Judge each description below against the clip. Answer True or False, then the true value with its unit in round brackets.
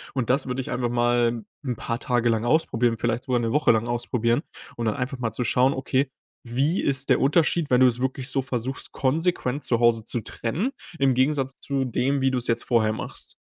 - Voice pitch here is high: False (125 Hz)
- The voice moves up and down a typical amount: False (2.3 semitones)